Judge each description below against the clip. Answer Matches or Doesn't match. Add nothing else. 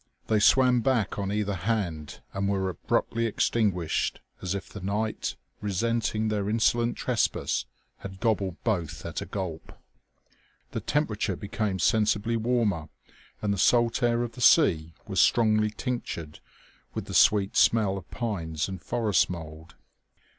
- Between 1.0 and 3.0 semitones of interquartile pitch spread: Doesn't match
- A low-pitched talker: Matches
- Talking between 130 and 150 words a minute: Matches